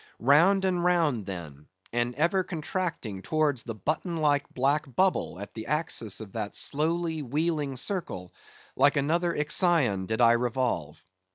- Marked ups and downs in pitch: Yes, wide, 6.5 semitones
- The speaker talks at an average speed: Yes, average, 145 wpm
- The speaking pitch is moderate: Yes, medium, 145 Hz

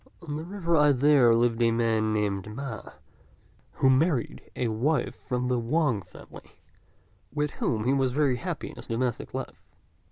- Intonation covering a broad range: No, average, 4.4 semitones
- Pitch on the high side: No, low, 125 Hz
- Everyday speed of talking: Yes, average, 165 wpm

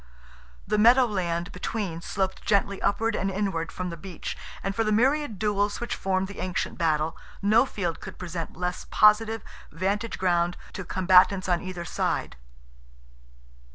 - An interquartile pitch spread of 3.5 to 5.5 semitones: No, average, 3.0 semitones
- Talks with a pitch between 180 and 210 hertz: Yes, high, 190 Hz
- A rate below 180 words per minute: Yes, average, 155 wpm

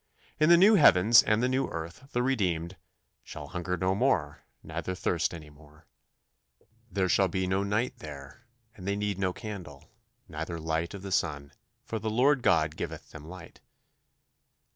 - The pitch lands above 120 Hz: No, very low, 95 Hz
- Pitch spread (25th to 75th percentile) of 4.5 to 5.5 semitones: Yes, average, 5.2 semitones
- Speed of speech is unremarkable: Yes, average, 165 wpm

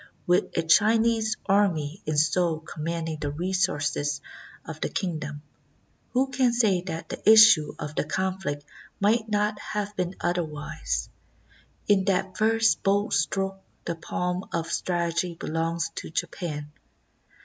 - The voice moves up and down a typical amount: Yes, average, 4.6 semitones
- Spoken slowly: Yes, slow, 130 wpm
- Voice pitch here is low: No, medium, 180 Hz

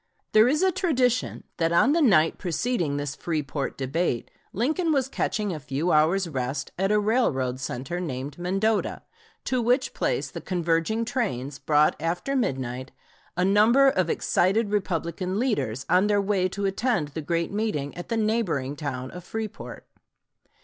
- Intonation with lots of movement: Yes, wide, 7.1 semitones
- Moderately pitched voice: Yes, medium, 180 Hz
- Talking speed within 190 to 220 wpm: No, average, 155 wpm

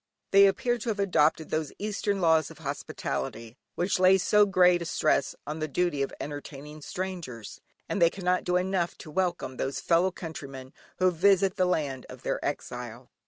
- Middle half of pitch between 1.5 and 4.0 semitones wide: No, average, 4.4 semitones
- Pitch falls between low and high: Yes, medium, 170 Hz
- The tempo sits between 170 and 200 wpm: Yes, average, 175 wpm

